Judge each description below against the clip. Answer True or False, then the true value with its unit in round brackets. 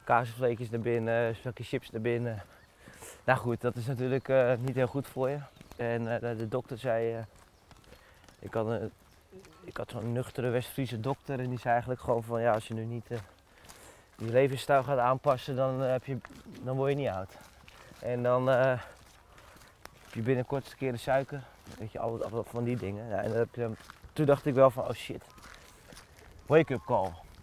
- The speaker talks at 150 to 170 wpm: False (195 wpm)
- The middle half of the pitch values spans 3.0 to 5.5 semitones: False (2.5 semitones)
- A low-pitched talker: True (120 Hz)